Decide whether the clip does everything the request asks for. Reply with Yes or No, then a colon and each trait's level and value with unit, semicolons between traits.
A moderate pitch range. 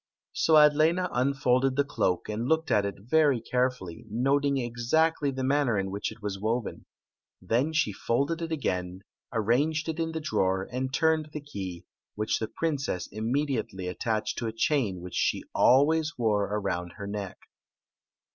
No: wide, 6.1 semitones